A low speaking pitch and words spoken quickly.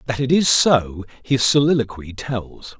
No: low, 120 Hz; average, 150 wpm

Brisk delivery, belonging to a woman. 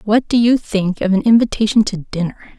Yes: fast, 210 wpm; female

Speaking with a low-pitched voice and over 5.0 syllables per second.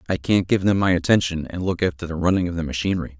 Yes: very low, 85 Hz; 7.0 syllables/s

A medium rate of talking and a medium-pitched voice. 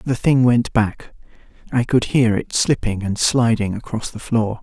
No: average, 170 wpm; low, 115 Hz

